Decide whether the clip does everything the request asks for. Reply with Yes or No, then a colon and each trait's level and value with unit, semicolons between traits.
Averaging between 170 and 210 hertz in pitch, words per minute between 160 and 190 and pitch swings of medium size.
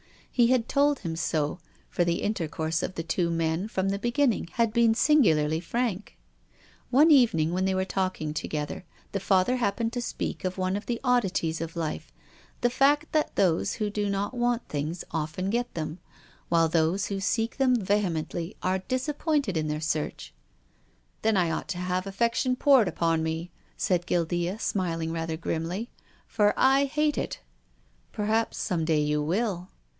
No: high, 190 Hz; average, 175 wpm; wide, 6.2 semitones